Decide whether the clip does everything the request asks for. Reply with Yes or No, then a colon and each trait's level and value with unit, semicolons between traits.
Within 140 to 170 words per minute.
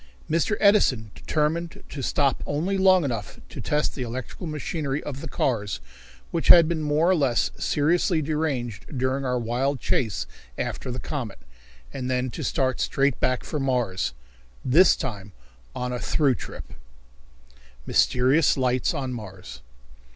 Yes: average, 145 wpm